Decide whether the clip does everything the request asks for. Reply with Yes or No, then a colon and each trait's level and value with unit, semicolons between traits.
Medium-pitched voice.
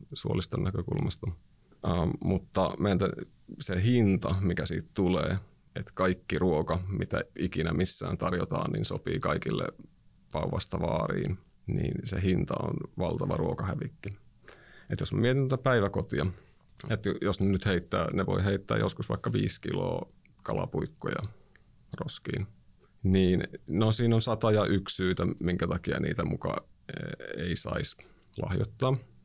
No: very low, 95 Hz